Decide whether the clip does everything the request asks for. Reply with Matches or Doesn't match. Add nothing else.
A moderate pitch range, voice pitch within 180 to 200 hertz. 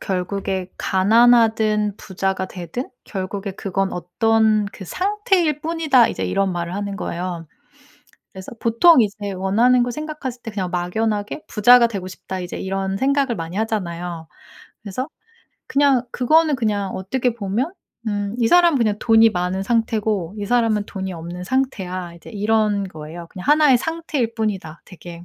Doesn't match